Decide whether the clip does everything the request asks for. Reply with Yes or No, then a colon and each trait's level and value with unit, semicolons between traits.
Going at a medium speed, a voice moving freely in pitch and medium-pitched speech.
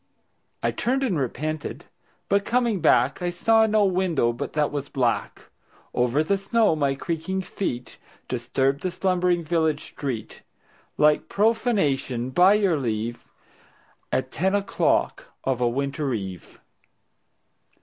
No: slow, 130 wpm; wide, 6.6 semitones; medium, 155 Hz